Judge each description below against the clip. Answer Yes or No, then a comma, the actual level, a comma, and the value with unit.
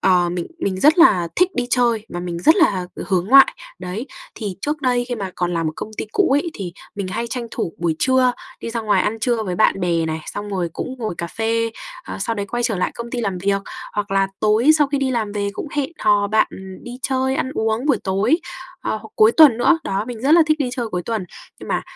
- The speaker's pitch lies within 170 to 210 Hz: No, high, 220 Hz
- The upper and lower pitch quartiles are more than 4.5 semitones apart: Yes, average, 4.9 semitones